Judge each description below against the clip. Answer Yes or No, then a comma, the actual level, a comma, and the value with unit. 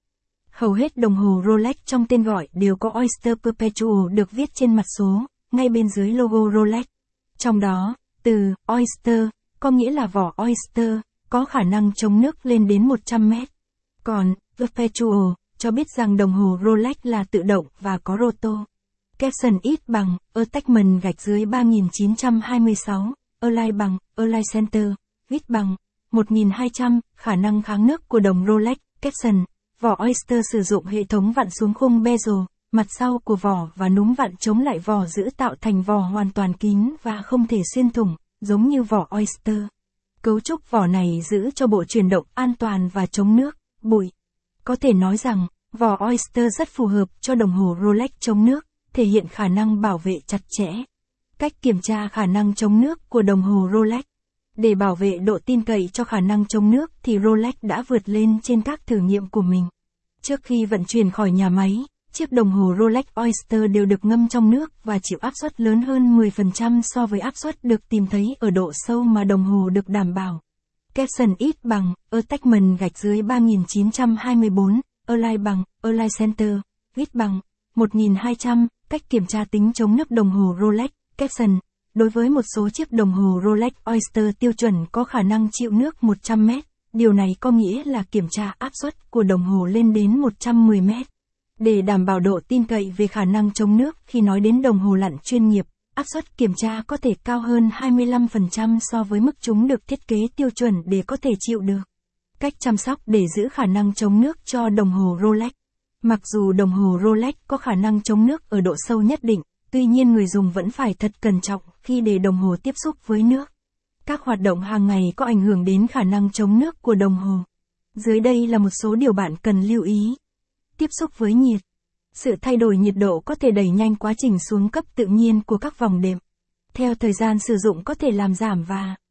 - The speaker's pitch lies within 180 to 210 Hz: No, high, 220 Hz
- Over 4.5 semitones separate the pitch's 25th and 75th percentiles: No, average, 3.0 semitones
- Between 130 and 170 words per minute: No, average, 200 wpm